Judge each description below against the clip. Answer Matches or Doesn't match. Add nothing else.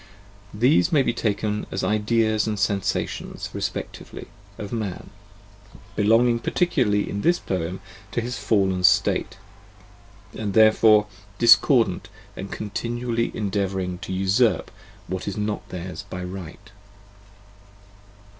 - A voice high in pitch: Doesn't match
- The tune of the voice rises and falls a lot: Doesn't match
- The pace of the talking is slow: Matches